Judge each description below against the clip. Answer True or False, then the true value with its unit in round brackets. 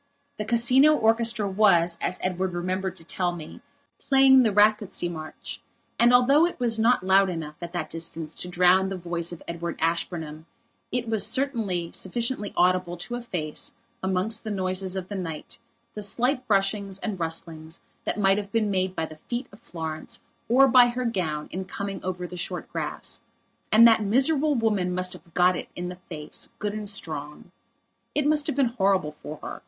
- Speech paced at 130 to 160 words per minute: False (180 wpm)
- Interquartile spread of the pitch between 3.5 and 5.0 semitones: True (4.7 semitones)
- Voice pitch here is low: False (190 Hz)